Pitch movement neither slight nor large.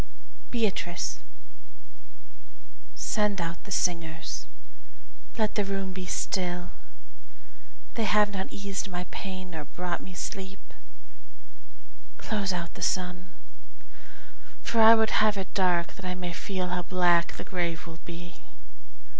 No: narrow, 2.2 semitones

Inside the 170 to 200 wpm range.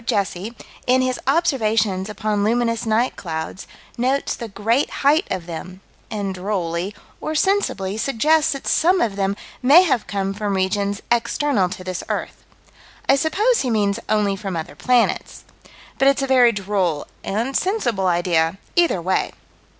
No: average, 150 wpm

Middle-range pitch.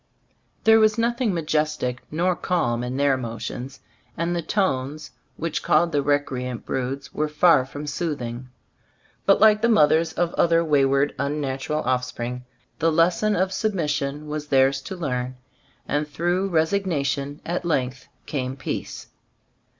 Yes: medium, 150 Hz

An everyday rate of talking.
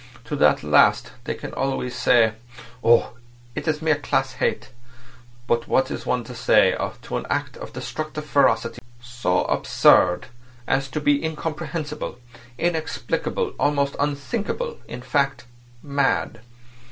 No: slow, 130 wpm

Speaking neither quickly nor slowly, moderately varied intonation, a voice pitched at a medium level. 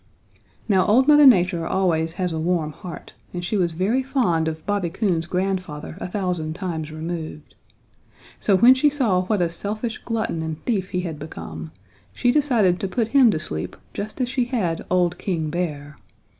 Yes: average, 180 wpm; average, 5.0 semitones; medium, 180 Hz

